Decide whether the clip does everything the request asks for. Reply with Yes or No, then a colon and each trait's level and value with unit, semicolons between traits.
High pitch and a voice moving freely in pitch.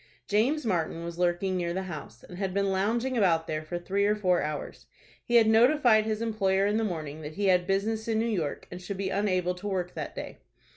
No: high, 195 Hz; average, 3.7 semitones